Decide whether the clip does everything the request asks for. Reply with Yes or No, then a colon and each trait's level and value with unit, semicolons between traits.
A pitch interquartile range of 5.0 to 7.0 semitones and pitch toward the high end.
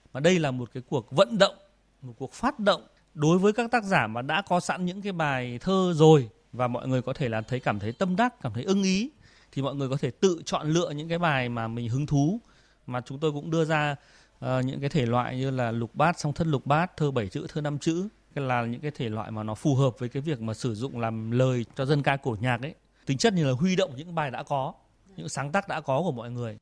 No: average, 5.3 semitones; medium, 145 Hz